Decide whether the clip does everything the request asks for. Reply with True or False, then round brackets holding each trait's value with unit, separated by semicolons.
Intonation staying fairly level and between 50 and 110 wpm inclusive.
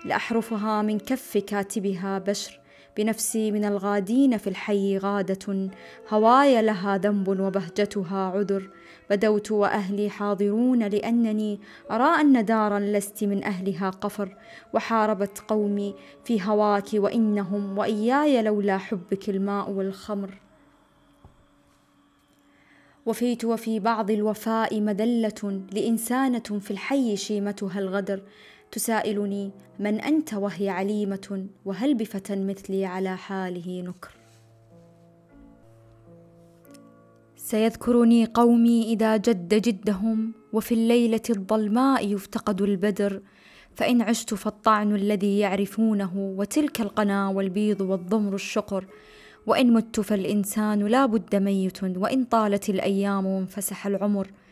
True (2.1 semitones; 100 wpm)